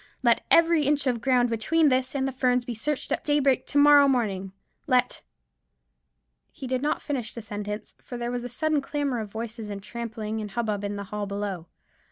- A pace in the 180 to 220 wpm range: Yes, average, 200 wpm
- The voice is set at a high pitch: Yes, high, 245 Hz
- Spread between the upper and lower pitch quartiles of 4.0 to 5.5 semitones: Yes, average, 4.5 semitones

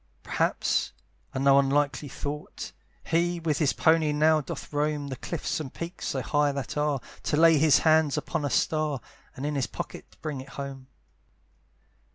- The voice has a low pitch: No, medium, 150 Hz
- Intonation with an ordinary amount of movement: No, narrow, 2.1 semitones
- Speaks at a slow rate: No, average, 170 wpm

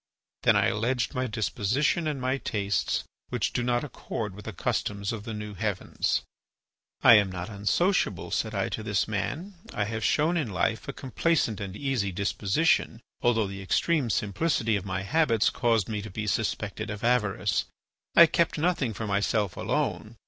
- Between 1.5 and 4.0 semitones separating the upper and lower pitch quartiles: No, average, 4.4 semitones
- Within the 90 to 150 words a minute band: No, average, 170 wpm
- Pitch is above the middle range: No, low, 110 Hz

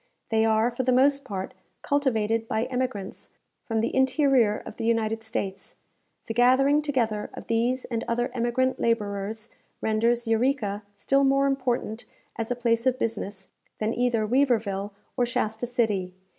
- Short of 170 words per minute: Yes, average, 150 wpm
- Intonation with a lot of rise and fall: No, average, 2.7 semitones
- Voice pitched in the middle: No, high, 230 Hz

